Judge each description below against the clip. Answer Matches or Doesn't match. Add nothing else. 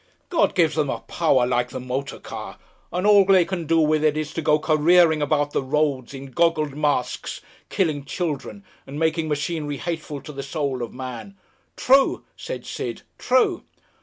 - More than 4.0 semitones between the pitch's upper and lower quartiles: Doesn't match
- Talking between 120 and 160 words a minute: Doesn't match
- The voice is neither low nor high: Matches